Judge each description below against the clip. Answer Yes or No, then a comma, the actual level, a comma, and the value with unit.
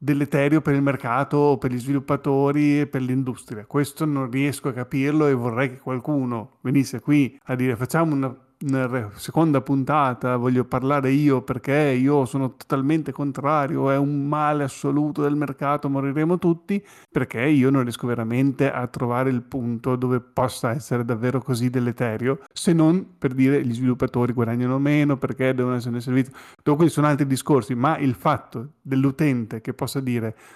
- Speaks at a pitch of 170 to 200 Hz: No, low, 135 Hz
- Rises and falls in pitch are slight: Yes, narrow, 2.3 semitones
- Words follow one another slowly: No, average, 165 wpm